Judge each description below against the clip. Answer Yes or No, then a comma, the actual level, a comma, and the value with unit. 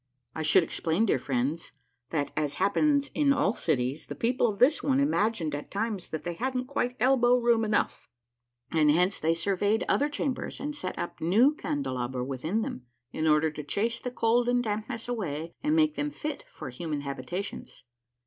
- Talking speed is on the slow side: No, average, 180 wpm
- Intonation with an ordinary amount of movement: No, wide, 8.1 semitones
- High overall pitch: Yes, high, 205 Hz